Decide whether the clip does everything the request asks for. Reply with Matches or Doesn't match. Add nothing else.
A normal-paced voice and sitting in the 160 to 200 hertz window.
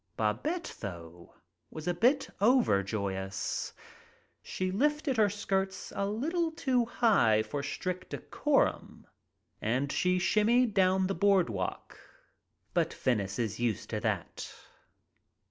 Doesn't match